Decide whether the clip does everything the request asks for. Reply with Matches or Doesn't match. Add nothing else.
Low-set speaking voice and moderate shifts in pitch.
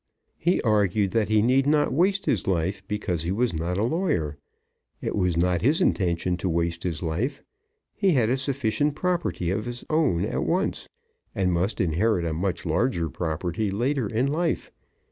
Doesn't match